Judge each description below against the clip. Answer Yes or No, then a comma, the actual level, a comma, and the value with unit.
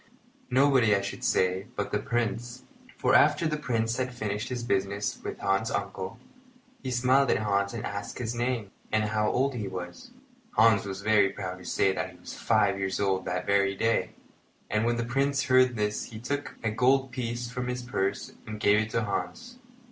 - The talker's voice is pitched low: Yes, low, 110 Hz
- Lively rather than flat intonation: No, average, 3.9 semitones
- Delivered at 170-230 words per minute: Yes, average, 195 wpm